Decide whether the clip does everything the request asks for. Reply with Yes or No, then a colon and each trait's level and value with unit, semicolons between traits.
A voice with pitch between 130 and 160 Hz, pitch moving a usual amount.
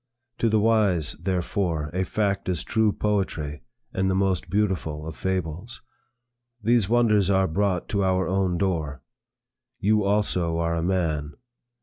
No: very low, 95 Hz; average, 3.6 semitones